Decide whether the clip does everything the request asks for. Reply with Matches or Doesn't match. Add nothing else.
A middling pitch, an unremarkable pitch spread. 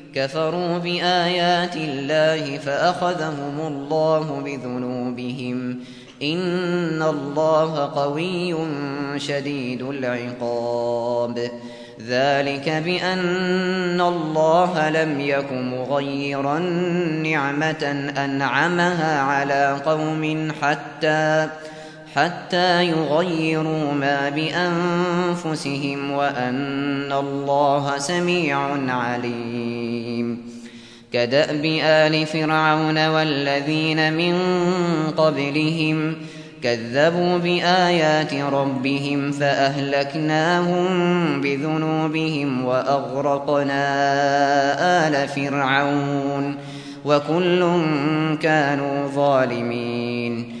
Doesn't match